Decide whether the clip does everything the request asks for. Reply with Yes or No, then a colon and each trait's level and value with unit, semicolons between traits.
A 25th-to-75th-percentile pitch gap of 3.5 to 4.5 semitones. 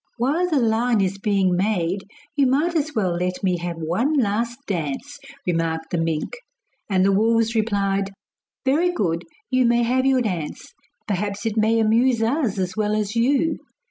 No: average, 5.1 semitones